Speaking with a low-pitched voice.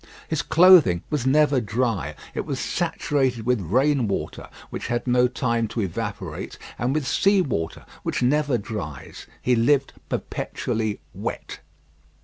Yes: low, 125 Hz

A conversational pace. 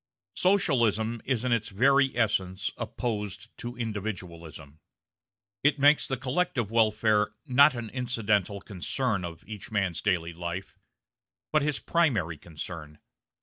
No: slow, 120 wpm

